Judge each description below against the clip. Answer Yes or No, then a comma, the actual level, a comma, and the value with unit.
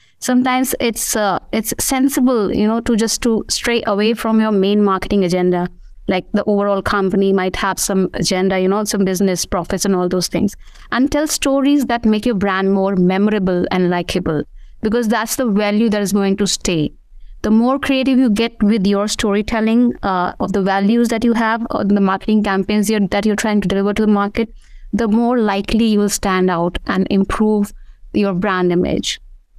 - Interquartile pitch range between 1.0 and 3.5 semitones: Yes, average, 3.0 semitones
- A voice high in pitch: Yes, high, 205 Hz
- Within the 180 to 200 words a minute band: Yes, average, 190 wpm